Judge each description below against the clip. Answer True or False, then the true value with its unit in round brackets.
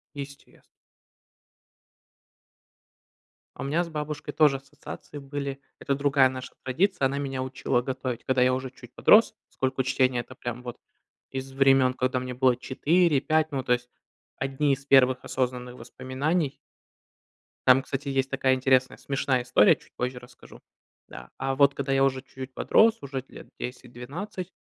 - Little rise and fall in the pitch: True (1.6 semitones)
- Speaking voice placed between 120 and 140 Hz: True (135 Hz)